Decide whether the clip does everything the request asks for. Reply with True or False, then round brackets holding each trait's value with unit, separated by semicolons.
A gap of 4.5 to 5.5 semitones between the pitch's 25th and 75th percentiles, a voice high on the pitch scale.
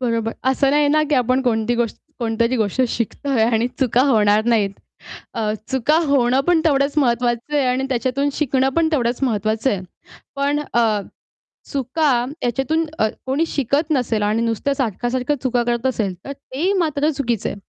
False (3.4 semitones; 250 Hz)